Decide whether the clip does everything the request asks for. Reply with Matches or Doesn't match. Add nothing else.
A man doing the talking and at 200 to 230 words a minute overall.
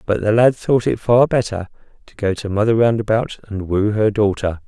Matches